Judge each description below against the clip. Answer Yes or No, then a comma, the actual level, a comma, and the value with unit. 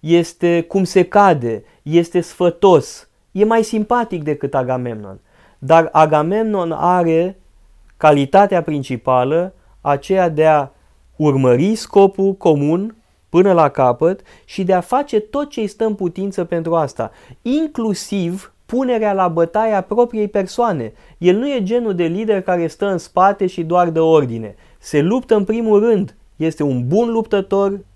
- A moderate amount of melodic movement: Yes, average, 4.7 semitones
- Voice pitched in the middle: Yes, medium, 180 Hz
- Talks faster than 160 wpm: No, average, 140 wpm